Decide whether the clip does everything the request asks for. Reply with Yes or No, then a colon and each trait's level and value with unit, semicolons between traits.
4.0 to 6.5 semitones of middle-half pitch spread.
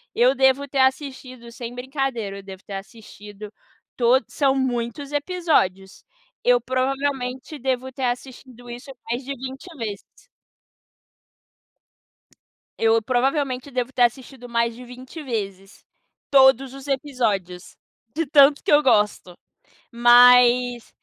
No: narrow, 2.4 semitones